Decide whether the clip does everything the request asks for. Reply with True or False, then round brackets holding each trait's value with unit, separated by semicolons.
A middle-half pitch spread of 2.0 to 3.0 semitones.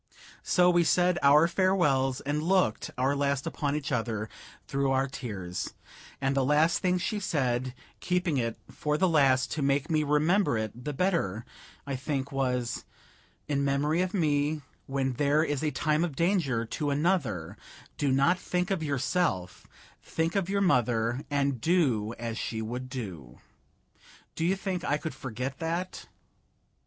False (4.8 semitones)